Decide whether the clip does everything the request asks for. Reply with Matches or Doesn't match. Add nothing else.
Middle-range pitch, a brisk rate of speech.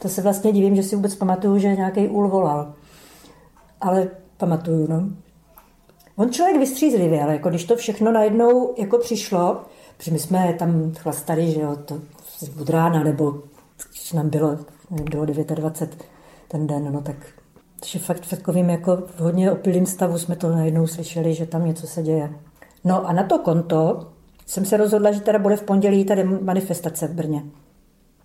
Matches